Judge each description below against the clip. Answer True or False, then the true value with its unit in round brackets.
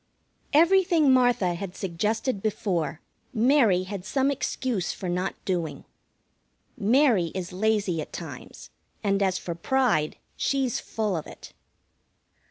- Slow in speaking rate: True (120 wpm)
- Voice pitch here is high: True (205 Hz)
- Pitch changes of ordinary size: False (6.2 semitones)